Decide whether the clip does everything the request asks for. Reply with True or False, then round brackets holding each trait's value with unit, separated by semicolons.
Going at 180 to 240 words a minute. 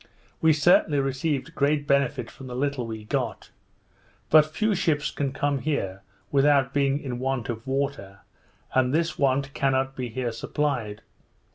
False (150 wpm)